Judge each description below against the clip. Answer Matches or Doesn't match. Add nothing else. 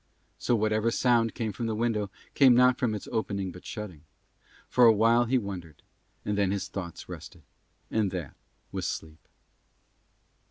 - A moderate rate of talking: Matches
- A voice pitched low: Matches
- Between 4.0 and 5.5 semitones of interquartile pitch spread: Doesn't match